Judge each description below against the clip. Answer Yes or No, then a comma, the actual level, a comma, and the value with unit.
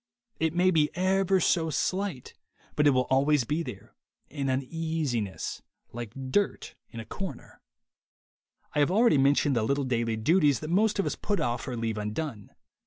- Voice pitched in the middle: Yes, medium, 145 Hz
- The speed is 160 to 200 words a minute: Yes, average, 170 wpm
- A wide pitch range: Yes, wide, 5.8 semitones